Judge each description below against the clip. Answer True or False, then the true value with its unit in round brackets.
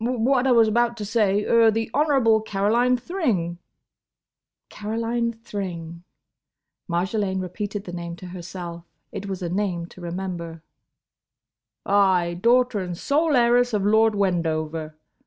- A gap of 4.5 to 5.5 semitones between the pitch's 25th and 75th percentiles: True (4.9 semitones)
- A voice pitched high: True (205 Hz)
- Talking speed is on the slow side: True (115 wpm)